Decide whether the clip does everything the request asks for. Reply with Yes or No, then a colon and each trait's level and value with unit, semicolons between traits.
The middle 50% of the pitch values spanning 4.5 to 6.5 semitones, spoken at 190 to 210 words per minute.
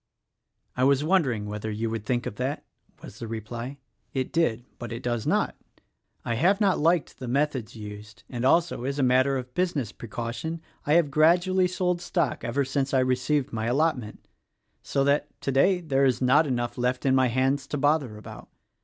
No: average, 4.1 semitones; average, 195 wpm